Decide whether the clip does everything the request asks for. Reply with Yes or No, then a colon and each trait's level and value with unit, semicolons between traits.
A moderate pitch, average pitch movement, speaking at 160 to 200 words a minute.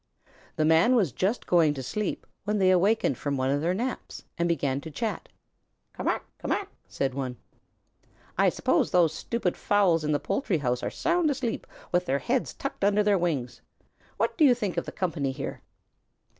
No: medium, 175 Hz; wide, 6.7 semitones; average, 190 wpm